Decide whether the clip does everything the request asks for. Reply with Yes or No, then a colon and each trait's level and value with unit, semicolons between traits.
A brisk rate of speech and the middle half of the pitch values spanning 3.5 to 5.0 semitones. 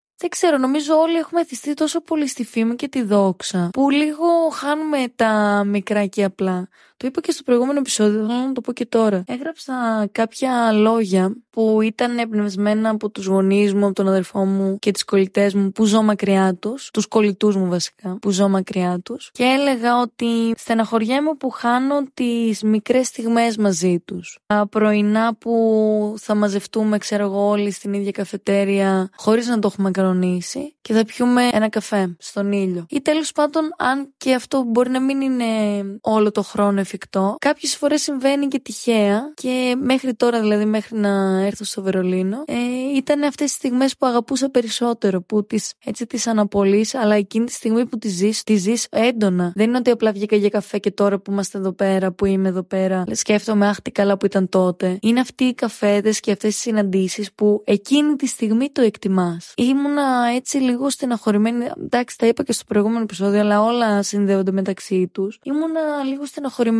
Yes: fast, 180 wpm; average, 3.9 semitones